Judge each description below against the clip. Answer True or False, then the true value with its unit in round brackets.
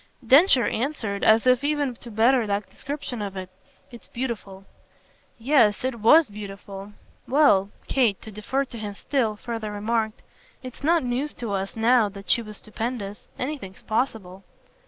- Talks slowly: False (155 wpm)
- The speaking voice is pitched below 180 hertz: False (225 Hz)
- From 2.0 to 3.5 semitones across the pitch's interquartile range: False (4.0 semitones)